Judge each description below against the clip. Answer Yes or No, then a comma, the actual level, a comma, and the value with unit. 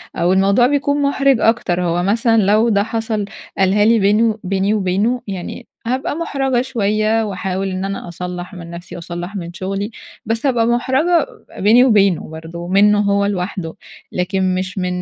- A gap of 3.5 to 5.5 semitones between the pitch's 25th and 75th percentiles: Yes, average, 3.8 semitones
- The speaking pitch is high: Yes, high, 200 Hz